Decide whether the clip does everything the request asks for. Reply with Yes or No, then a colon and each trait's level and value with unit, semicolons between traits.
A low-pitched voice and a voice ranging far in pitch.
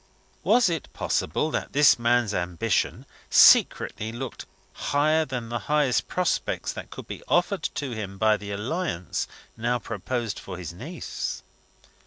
Yes: low, 120 Hz; wide, 6.5 semitones